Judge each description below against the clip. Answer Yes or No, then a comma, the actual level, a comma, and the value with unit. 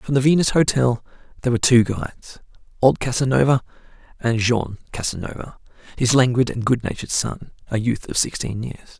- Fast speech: No, average, 155 wpm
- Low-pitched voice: Yes, low, 125 Hz